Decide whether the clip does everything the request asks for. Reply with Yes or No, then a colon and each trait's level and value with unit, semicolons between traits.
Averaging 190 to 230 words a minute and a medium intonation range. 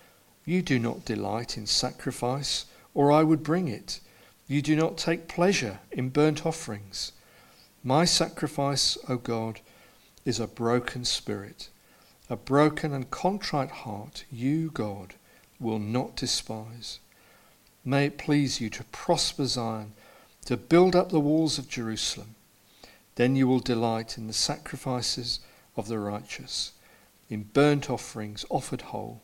No: average, 140 wpm; average, 4.8 semitones